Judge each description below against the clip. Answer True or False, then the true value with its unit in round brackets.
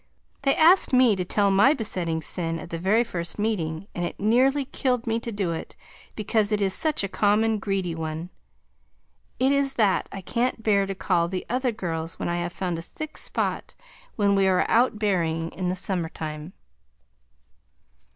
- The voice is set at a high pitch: True (195 Hz)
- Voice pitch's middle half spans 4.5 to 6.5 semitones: True (4.8 semitones)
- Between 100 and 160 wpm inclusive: False (185 wpm)